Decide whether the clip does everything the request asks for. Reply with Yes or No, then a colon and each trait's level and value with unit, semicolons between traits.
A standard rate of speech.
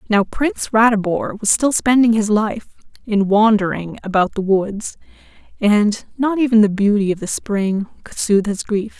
Yes: average, 165 wpm